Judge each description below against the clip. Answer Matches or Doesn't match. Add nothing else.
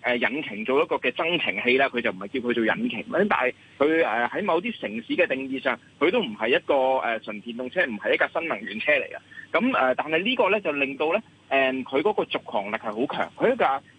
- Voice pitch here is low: Matches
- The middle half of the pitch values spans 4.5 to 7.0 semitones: Doesn't match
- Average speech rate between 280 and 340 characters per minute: Matches